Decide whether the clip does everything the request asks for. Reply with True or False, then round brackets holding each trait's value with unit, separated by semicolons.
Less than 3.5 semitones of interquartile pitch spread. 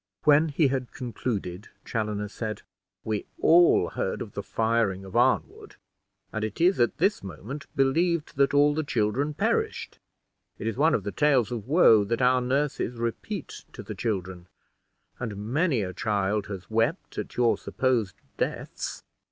False (5.4 semitones)